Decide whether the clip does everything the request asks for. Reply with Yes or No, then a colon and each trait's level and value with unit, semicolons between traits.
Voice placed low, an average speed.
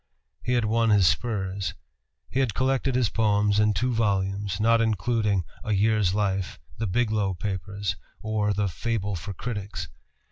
Yes: low, 105 Hz; average, 150 wpm